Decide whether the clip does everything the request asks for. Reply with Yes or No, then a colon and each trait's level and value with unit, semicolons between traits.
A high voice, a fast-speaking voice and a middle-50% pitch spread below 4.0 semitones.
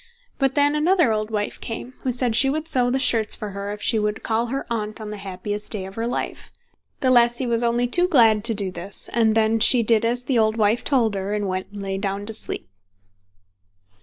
Yes: high, 225 Hz; fast, 230 wpm; average, 2.9 semitones